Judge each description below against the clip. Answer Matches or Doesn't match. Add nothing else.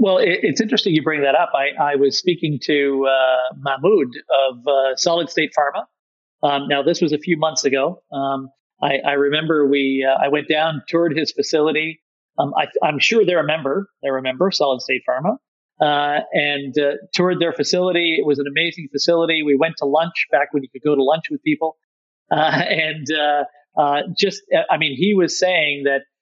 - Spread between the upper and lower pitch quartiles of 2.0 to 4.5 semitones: Matches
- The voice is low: Doesn't match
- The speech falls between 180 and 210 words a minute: Matches